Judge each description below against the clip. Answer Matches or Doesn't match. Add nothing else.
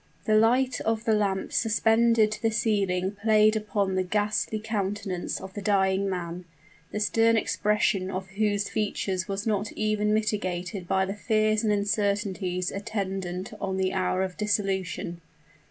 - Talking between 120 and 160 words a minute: Matches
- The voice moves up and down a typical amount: Doesn't match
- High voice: Matches